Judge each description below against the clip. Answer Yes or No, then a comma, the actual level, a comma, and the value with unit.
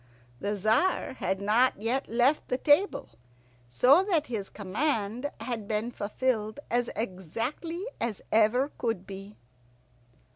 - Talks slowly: Yes, slow, 120 wpm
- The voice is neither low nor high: No, high, 230 Hz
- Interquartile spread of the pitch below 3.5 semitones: No, average, 4.2 semitones